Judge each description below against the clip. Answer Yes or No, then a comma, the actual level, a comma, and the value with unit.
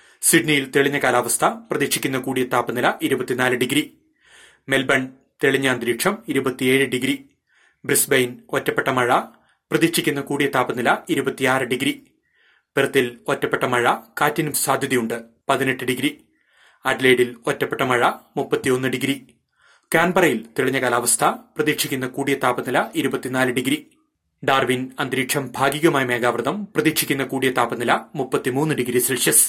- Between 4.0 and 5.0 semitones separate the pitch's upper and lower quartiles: No, average, 2.8 semitones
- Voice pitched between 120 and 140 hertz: Yes, low, 135 Hz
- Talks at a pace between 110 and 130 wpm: No, average, 100 wpm